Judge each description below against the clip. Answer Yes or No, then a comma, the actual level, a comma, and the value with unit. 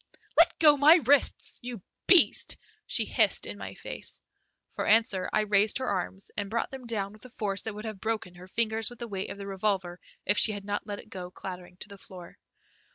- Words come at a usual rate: No, fast, 220 wpm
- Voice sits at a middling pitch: No, high, 205 Hz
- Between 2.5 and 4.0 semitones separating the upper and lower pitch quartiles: Yes, average, 2.8 semitones